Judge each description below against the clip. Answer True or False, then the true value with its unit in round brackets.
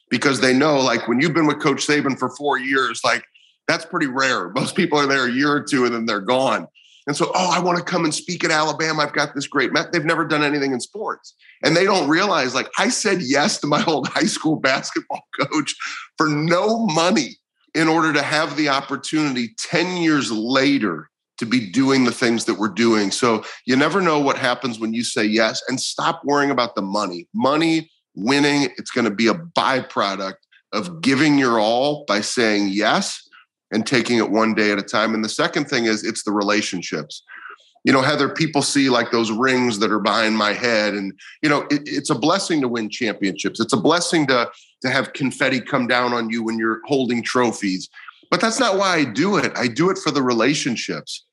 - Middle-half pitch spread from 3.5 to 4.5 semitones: False (5.2 semitones)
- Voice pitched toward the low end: True (130 Hz)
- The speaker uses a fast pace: True (215 wpm)